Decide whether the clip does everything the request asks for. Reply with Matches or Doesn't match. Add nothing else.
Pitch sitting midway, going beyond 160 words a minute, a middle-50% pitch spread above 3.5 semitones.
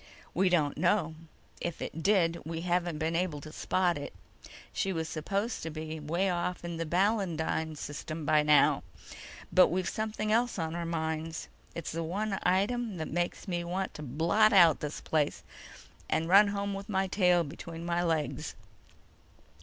Doesn't match